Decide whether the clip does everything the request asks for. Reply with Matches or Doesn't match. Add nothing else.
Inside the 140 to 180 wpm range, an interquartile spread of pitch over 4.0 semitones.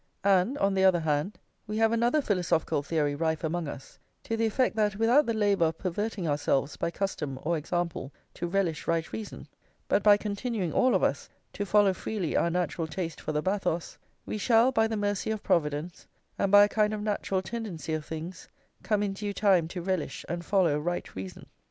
Doesn't match